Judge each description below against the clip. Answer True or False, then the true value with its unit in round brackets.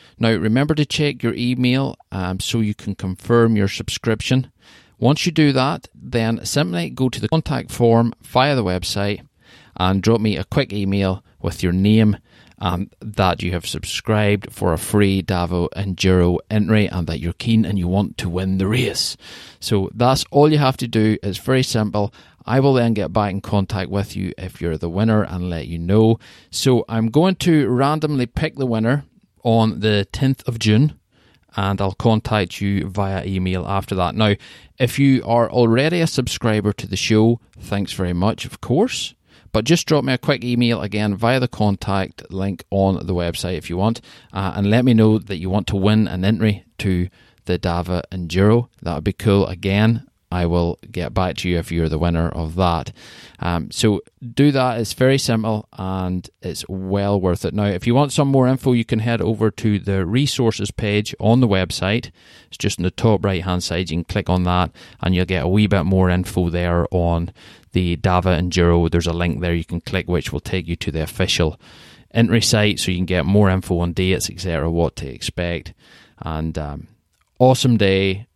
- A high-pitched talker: False (100 Hz)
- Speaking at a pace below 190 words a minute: False (200 wpm)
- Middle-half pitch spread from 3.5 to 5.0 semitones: True (4.2 semitones)